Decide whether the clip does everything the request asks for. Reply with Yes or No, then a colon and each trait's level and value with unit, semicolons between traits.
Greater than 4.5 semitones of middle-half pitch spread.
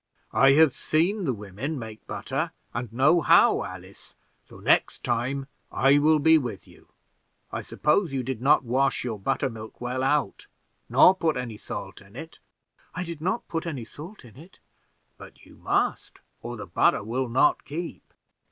Yes: average, 5.0 semitones